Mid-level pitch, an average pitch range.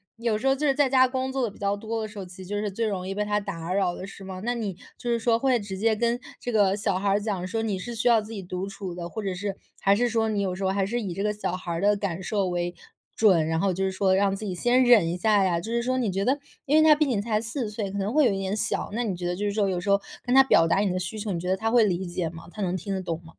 No: high, 200 Hz; average, 3.3 semitones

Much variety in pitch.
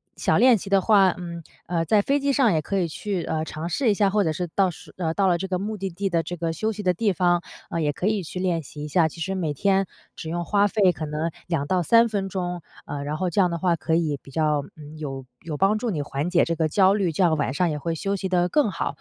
No: average, 3.6 semitones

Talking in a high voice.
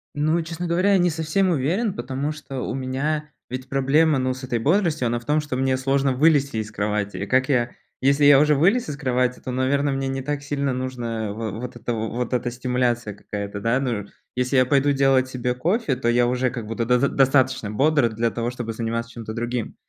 No: low, 130 Hz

